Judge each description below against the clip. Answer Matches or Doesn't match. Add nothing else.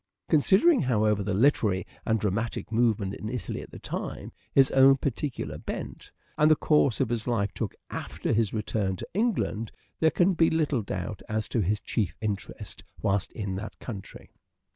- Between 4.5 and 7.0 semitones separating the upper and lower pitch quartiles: Matches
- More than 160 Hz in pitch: Doesn't match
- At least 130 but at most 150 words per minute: Doesn't match